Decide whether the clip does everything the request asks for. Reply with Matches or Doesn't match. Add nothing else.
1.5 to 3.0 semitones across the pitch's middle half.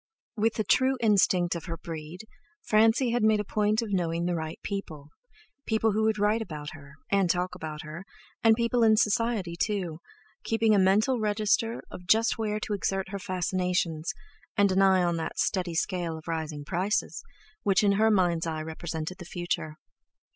Doesn't match